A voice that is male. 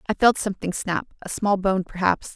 No: female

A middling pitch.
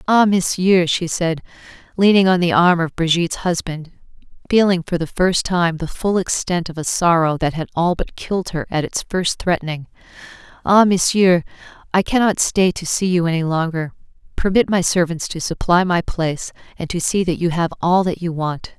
Yes: medium, 175 Hz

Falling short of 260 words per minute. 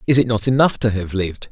No: fast, 275 wpm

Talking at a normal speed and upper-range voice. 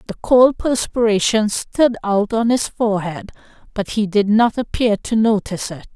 Yes: average, 160 wpm; high, 215 Hz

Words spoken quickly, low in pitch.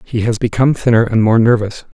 Yes: fast, 210 wpm; low, 115 Hz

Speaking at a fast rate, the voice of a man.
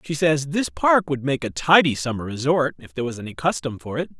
Yes: fast, 245 wpm; male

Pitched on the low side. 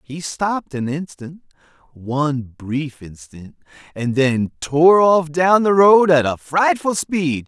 No: medium, 155 Hz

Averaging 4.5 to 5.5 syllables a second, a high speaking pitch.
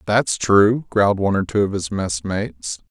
No: 5.0 syllables/s; low, 100 Hz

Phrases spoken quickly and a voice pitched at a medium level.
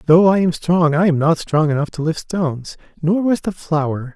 Yes: fast, 230 wpm; medium, 165 Hz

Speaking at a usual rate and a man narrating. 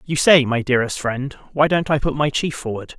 No: fast, 240 wpm; male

